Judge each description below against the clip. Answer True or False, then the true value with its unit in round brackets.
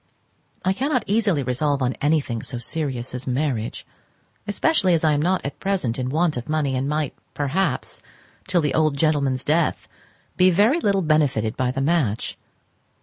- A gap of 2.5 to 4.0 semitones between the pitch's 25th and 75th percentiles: False (5.3 semitones)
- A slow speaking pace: False (165 wpm)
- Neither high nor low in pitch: True (150 Hz)